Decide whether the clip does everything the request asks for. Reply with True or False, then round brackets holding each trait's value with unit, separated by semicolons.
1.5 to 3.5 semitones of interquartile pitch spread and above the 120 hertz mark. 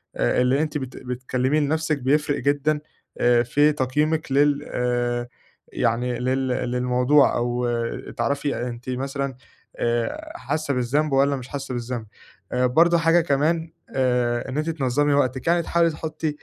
True (3.2 semitones; 135 Hz)